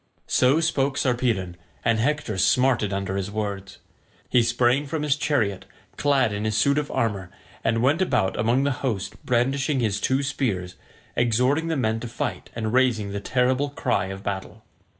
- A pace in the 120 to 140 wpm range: No, average, 170 wpm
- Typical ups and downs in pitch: Yes, average, 4.9 semitones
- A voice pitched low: Yes, low, 120 Hz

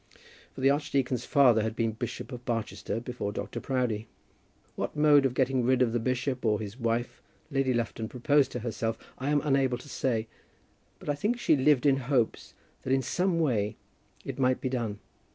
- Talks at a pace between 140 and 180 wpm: No, average, 190 wpm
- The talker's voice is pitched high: No, low, 125 Hz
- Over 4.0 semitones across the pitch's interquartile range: No, average, 3.0 semitones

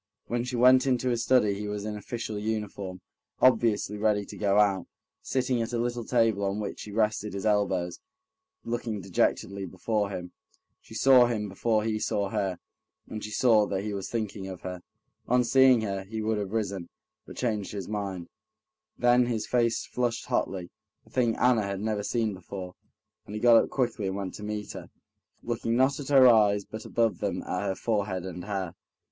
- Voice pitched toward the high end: No, low, 105 Hz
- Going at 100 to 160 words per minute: No, average, 190 wpm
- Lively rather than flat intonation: No, average, 3.0 semitones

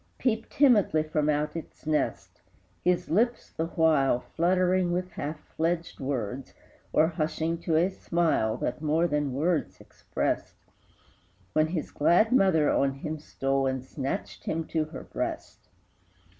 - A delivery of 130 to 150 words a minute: Yes, average, 140 wpm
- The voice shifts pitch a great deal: No, average, 3.1 semitones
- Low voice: No, medium, 160 Hz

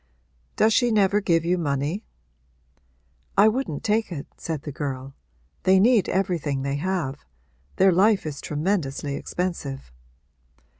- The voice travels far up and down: Yes, wide, 5.8 semitones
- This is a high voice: No, medium, 170 Hz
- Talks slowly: Yes, slow, 130 wpm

